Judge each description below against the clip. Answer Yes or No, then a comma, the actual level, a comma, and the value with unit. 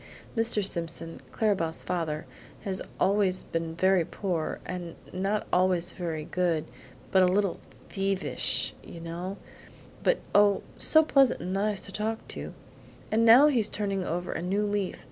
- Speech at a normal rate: Yes, average, 150 wpm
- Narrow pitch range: No, average, 3.2 semitones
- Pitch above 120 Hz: Yes, high, 190 Hz